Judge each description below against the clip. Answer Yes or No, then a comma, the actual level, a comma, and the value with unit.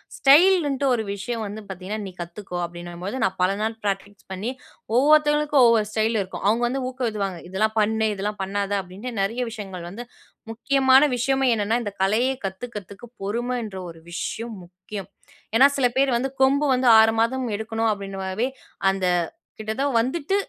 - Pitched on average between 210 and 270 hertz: Yes, high, 220 Hz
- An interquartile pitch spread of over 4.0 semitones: Yes, average, 4.4 semitones